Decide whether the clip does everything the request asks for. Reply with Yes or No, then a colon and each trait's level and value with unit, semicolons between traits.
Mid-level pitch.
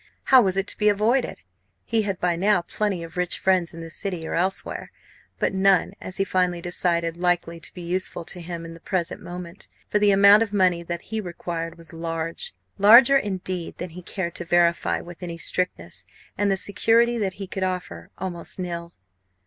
Yes: medium, 180 Hz